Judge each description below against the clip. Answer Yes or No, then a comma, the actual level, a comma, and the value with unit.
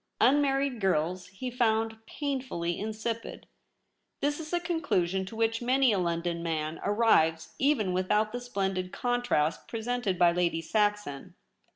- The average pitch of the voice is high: Yes, high, 215 Hz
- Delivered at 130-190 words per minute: Yes, average, 140 wpm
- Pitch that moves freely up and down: Yes, wide, 5.7 semitones